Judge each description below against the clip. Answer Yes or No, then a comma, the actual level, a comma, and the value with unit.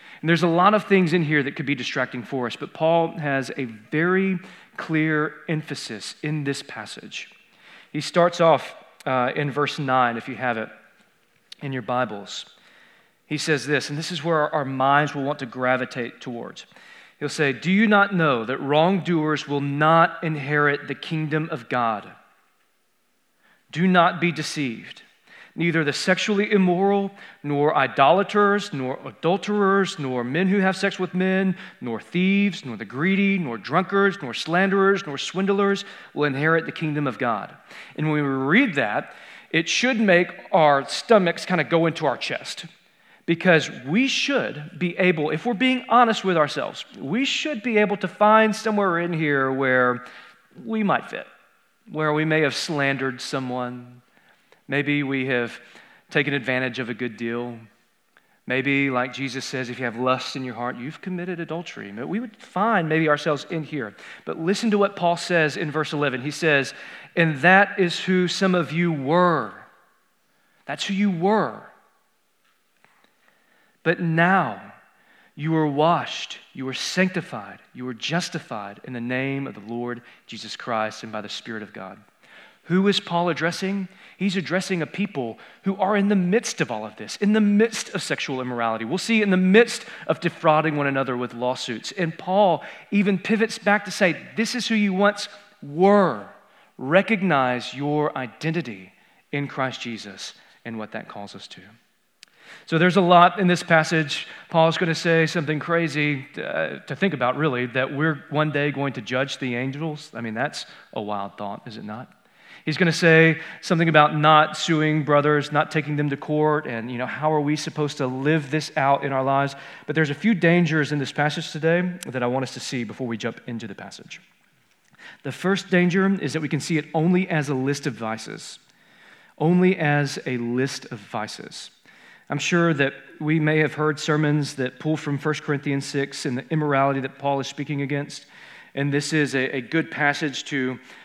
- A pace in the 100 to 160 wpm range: No, average, 180 wpm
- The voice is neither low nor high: Yes, medium, 155 Hz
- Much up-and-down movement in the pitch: No, average, 5.0 semitones